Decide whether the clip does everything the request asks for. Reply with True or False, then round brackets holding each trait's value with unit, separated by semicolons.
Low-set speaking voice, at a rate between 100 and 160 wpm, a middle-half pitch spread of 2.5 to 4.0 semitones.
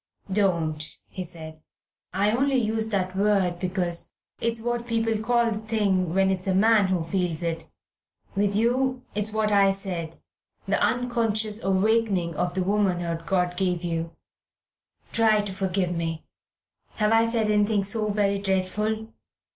False (200 Hz; 145 wpm; 3.4 semitones)